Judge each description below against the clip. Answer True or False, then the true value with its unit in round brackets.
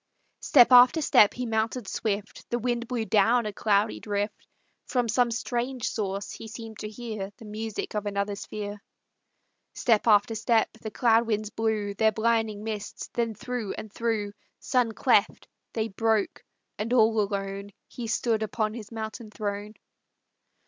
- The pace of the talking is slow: False (155 wpm)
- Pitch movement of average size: False (2.0 semitones)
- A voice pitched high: True (220 Hz)